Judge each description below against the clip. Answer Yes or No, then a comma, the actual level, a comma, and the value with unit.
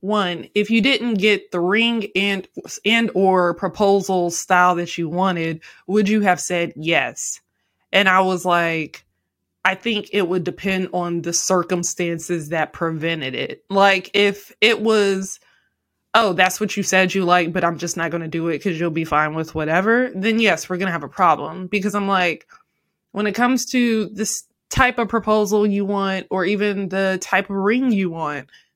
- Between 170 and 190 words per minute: Yes, average, 185 wpm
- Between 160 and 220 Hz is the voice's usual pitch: Yes, high, 190 Hz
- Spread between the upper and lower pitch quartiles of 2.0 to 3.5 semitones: Yes, average, 3.2 semitones